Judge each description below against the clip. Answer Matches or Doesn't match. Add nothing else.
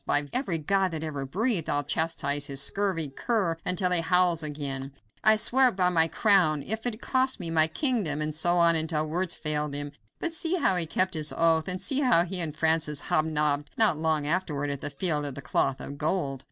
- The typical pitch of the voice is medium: Matches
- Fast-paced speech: Matches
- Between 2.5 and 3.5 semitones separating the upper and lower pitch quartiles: Doesn't match